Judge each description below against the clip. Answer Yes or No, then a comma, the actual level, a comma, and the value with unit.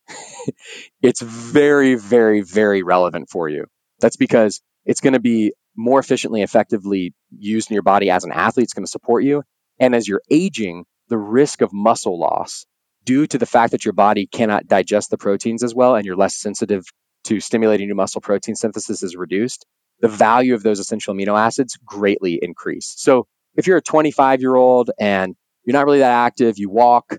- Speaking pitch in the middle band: No, low, 110 Hz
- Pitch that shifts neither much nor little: Yes, average, 3.8 semitones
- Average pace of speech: Yes, average, 190 wpm